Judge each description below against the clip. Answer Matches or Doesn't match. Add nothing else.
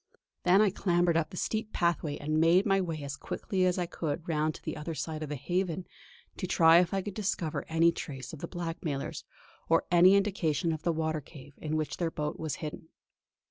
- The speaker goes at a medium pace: Doesn't match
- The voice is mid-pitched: Matches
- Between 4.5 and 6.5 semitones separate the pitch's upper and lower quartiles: Doesn't match